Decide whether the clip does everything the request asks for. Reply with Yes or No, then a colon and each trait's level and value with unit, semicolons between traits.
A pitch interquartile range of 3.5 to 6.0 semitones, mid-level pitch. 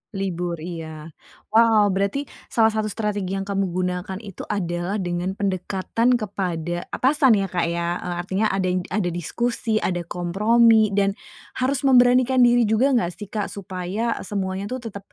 No: average, 3.8 semitones; high, 195 Hz